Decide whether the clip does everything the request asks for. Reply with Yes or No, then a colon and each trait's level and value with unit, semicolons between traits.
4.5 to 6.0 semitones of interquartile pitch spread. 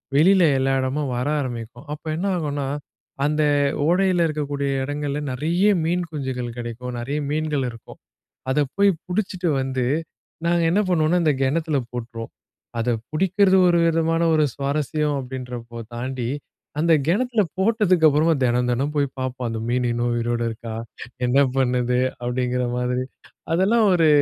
Yes: average, 5.0 semitones